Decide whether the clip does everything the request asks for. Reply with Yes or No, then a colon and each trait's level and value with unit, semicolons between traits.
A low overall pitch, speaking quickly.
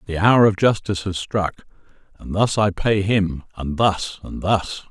No: very low, 95 Hz; average, 160 wpm